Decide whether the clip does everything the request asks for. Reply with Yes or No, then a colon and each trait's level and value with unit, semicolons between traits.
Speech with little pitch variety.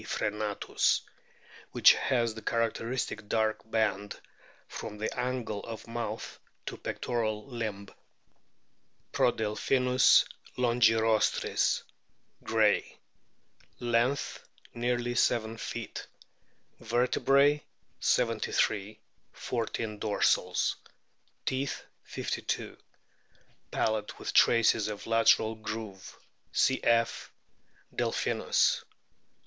Yes: narrow, 2.0 semitones